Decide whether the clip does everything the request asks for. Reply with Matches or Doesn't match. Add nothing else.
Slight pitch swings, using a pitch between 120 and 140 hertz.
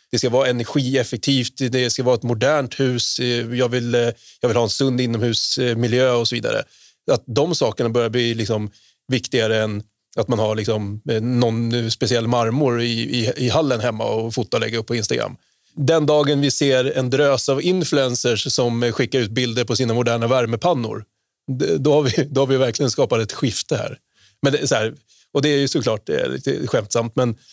Matches